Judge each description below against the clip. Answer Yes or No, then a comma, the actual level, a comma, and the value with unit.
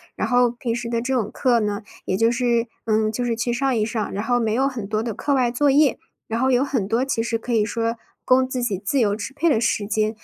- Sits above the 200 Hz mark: Yes, high, 235 Hz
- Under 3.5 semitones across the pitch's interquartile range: Yes, narrow, 2.5 semitones